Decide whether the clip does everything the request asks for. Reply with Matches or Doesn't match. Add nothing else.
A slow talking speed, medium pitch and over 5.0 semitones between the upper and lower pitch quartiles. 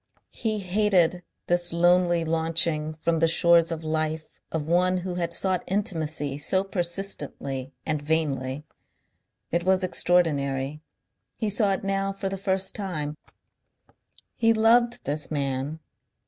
Doesn't match